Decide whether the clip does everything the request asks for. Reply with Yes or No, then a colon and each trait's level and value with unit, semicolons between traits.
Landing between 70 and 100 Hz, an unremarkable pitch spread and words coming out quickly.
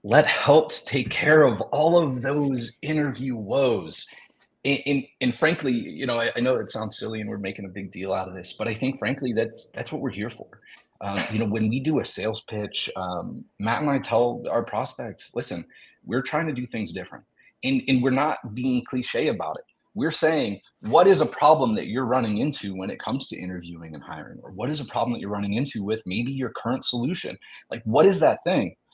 No: low, 125 Hz; average, 3.9 semitones; fast, 225 wpm